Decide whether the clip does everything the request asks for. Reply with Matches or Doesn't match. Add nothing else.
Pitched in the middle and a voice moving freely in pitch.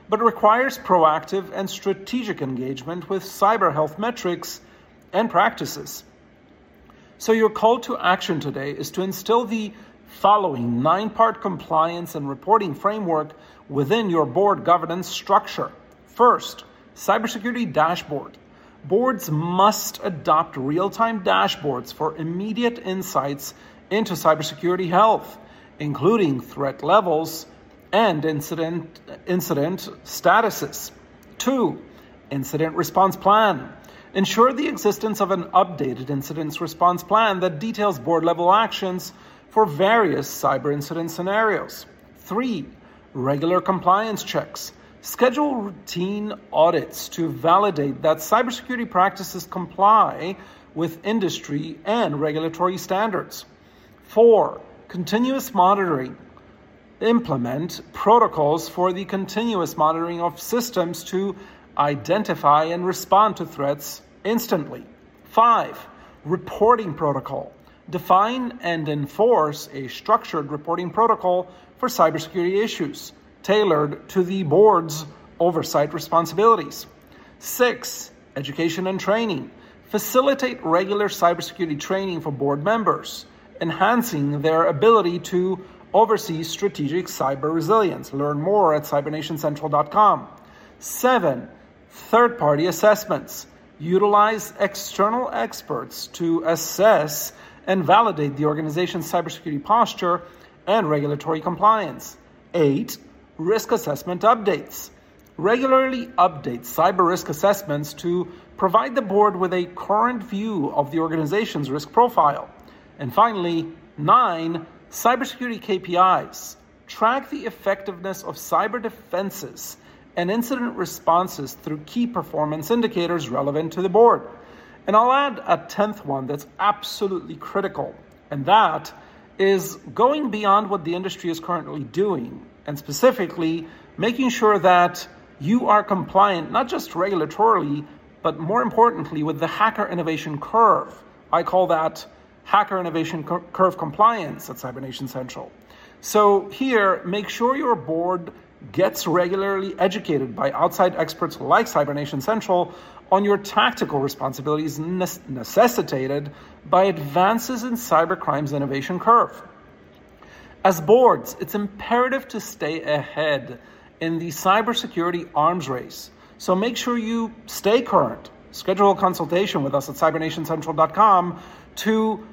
Doesn't match